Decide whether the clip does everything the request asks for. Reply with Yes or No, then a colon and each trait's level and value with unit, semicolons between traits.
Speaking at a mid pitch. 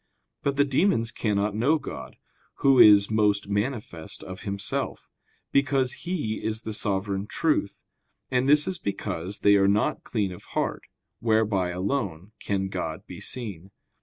No: low, 105 Hz